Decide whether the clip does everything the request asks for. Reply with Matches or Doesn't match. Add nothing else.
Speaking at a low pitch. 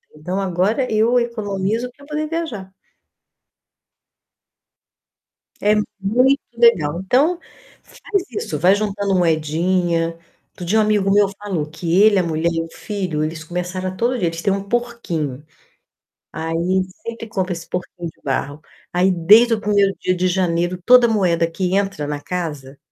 Doesn't match